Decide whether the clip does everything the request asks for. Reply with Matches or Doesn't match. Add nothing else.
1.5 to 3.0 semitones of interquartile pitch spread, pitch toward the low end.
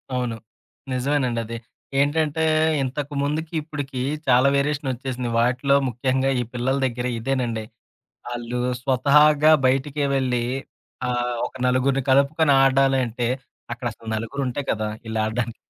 Matches